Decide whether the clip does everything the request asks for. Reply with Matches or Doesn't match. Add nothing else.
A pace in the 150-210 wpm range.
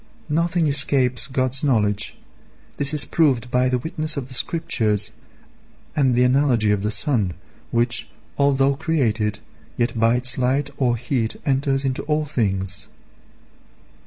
Doesn't match